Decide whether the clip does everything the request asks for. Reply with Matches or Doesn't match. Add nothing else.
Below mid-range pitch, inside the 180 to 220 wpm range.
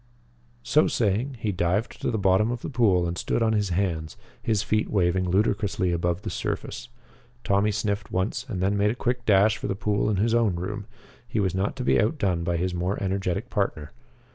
Matches